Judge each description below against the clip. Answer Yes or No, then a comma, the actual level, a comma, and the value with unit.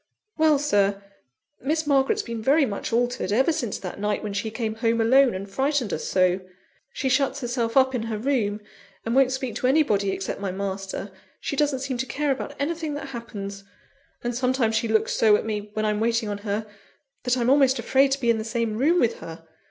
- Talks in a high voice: Yes, high, 235 Hz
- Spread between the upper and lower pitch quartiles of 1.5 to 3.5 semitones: No, average, 4.4 semitones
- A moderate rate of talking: No, fast, 210 wpm